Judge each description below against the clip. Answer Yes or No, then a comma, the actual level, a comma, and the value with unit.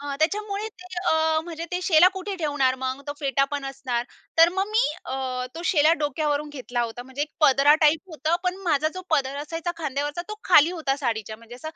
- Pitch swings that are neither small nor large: Yes, average, 3.8 semitones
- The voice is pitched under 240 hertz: No, very high, 300 Hz